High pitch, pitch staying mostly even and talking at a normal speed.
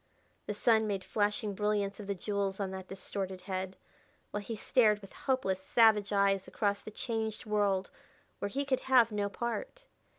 Yes: high, 205 Hz; narrow, 2.1 semitones; average, 170 wpm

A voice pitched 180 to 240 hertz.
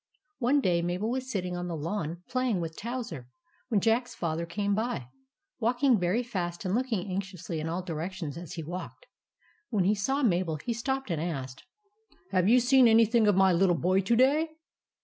Yes: high, 190 Hz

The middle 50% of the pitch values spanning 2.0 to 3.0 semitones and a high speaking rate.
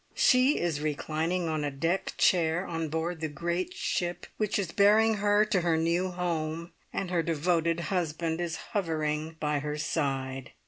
No: narrow, 2.5 semitones; average, 165 wpm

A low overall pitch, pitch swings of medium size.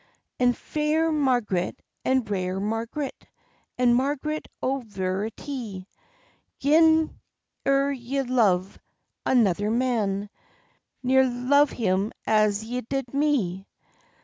No: high, 245 Hz; average, 5.0 semitones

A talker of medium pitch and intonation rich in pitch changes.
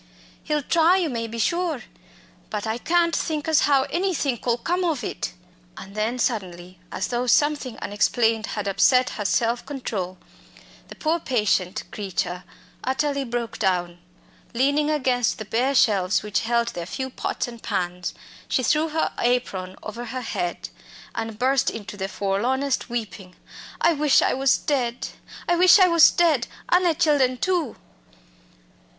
No: high, 245 Hz; wide, 5.9 semitones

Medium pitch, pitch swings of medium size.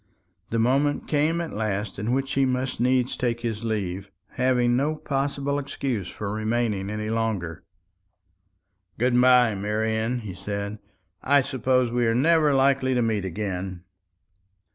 No: low, 120 Hz; average, 3.8 semitones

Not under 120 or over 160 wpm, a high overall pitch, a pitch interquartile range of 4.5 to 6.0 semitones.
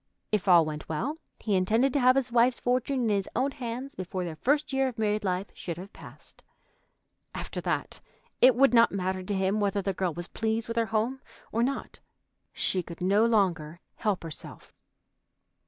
No: average, 190 wpm; high, 215 Hz; average, 4.9 semitones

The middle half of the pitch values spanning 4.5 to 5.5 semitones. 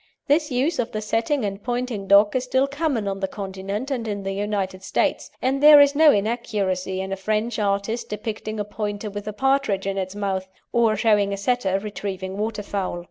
No: average, 3.7 semitones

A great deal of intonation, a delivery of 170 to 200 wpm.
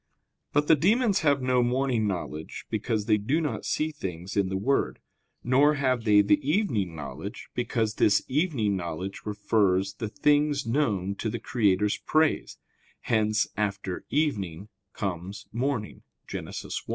No: wide, 6.1 semitones; average, 145 wpm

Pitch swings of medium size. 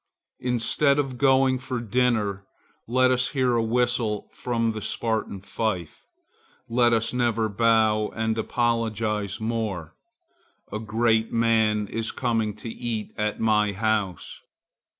No: narrow, 2.1 semitones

